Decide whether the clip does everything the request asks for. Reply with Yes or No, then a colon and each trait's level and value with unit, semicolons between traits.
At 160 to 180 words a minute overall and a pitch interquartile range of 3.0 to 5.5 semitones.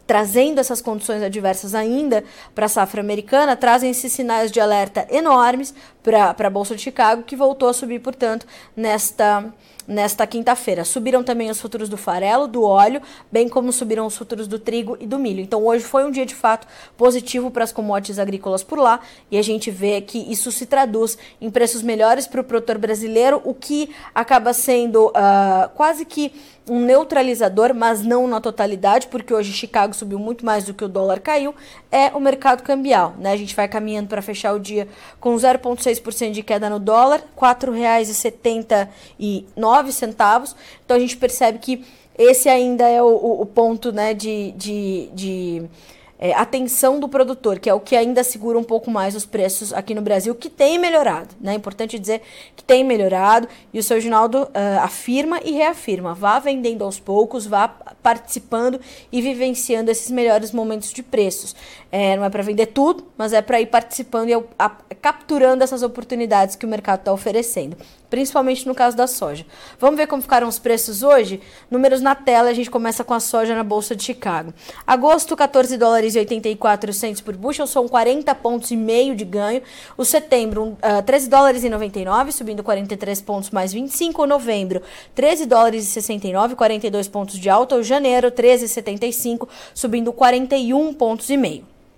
Yes: average, 175 wpm; average, 3.3 semitones